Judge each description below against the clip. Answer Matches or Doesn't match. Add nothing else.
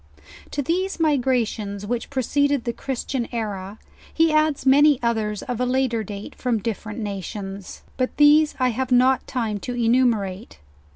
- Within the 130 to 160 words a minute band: Matches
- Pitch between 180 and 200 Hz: Doesn't match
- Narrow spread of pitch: Doesn't match